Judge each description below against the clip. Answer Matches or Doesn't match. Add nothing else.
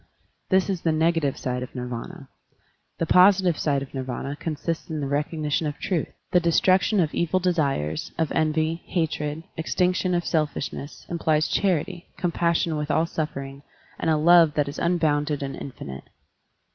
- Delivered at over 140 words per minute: Matches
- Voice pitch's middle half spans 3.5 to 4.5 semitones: Doesn't match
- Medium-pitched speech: Matches